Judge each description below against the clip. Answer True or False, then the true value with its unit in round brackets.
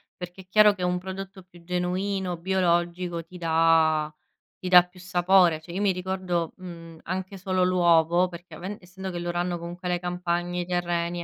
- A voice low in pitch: False (180 Hz)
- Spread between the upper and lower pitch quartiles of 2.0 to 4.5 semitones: False (1.3 semitones)